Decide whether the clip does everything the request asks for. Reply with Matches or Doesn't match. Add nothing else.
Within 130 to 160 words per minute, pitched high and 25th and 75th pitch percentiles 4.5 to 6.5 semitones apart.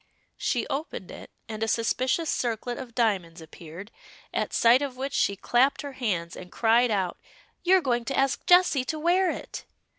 Doesn't match